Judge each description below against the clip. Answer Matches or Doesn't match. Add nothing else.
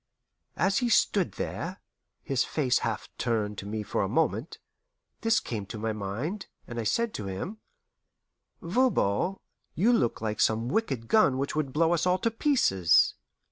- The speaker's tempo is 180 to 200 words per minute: Doesn't match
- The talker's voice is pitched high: Doesn't match